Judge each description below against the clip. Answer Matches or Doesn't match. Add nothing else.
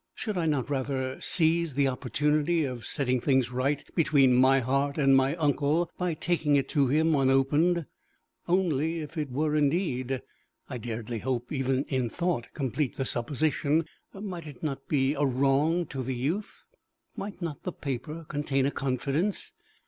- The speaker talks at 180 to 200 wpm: Doesn't match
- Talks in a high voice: Doesn't match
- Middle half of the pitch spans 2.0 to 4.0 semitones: Matches